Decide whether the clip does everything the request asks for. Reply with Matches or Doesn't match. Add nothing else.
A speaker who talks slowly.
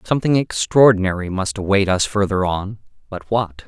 Doesn't match